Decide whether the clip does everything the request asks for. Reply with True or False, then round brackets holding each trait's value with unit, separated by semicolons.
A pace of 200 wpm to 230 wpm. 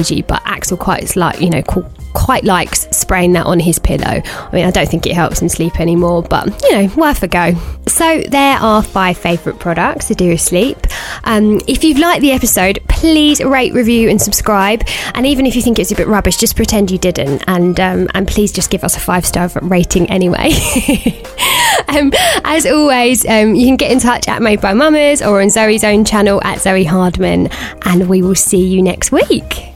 True (205 wpm)